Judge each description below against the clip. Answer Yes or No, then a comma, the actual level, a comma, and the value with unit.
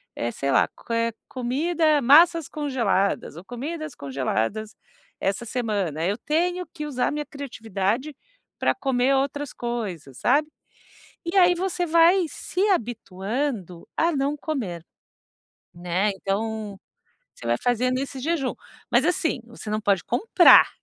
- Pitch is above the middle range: Yes, very high, 250 Hz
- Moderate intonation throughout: No, wide, 7.2 semitones